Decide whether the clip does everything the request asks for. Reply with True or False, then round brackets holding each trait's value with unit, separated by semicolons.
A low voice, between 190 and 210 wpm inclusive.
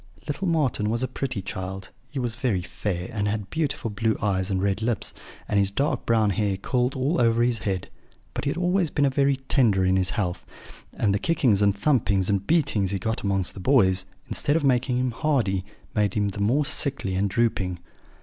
True (110 Hz; 205 wpm)